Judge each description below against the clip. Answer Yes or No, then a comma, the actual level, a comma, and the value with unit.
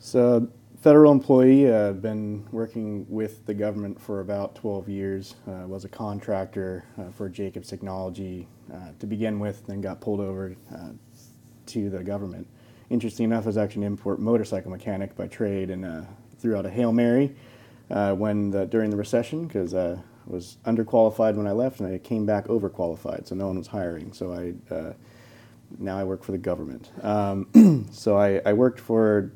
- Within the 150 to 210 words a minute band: Yes, average, 185 wpm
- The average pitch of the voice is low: Yes, low, 105 Hz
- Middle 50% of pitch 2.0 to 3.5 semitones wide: Yes, average, 3.1 semitones